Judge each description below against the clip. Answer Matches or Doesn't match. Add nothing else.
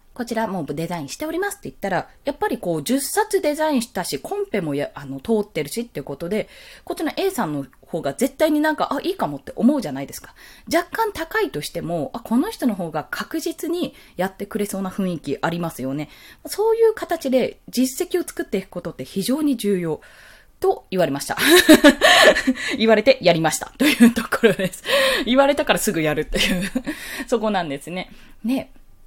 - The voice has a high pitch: Matches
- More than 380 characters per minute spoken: Matches